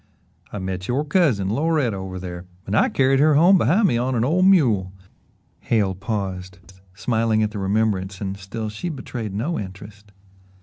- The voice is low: Yes, low, 110 Hz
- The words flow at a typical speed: Yes, average, 170 wpm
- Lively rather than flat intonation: Yes, wide, 5.9 semitones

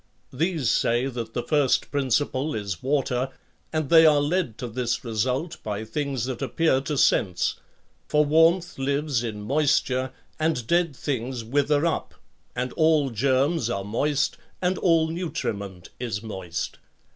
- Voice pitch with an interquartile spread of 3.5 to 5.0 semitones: Yes, average, 4.7 semitones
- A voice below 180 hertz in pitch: Yes, low, 135 Hz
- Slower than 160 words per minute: Yes, average, 145 wpm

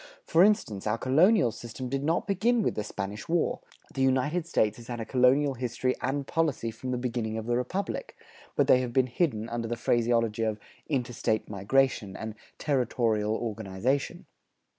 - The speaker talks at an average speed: Yes, average, 170 wpm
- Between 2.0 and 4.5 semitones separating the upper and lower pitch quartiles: Yes, average, 3.6 semitones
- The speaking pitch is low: Yes, low, 125 Hz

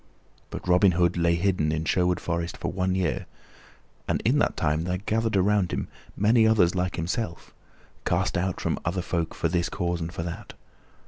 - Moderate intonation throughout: No, narrow, 2.0 semitones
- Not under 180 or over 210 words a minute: Yes, average, 185 wpm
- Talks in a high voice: No, very low, 90 Hz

